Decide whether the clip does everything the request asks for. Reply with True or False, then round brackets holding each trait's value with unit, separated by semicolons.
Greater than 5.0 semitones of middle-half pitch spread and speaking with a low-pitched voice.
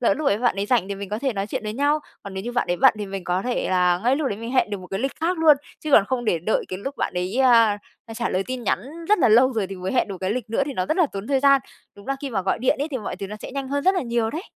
False (5.5 semitones; 230 Hz)